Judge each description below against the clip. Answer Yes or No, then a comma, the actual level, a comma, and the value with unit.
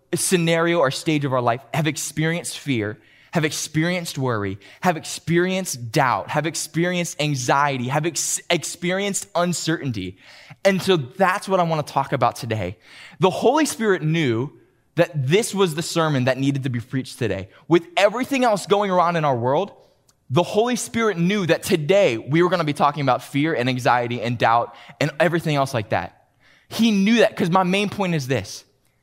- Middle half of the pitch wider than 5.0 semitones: Yes, wide, 5.4 semitones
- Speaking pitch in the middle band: Yes, medium, 160 Hz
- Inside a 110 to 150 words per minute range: No, average, 180 wpm